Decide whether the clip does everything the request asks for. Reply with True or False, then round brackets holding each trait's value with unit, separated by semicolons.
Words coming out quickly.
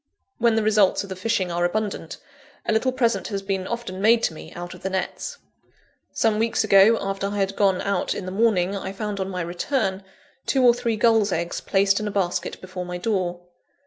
True (210 wpm)